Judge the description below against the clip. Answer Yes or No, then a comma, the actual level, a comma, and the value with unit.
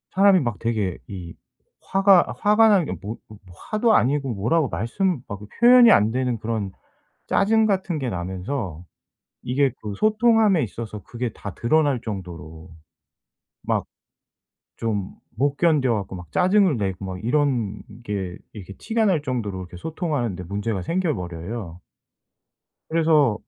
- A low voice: Yes, low, 120 Hz